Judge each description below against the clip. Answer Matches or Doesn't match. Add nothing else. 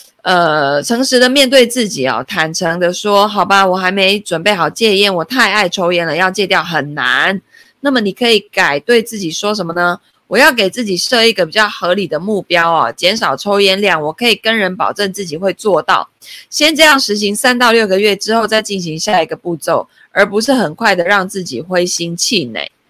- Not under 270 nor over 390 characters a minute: Matches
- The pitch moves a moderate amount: Matches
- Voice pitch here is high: Matches